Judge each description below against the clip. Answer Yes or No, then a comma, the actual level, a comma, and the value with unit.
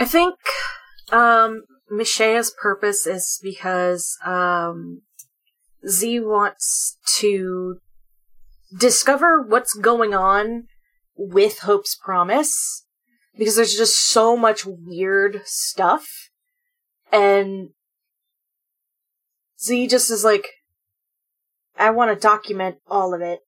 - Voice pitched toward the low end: No, high, 215 Hz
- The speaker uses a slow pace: Yes, slow, 95 wpm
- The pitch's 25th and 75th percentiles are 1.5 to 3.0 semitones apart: No, average, 4.5 semitones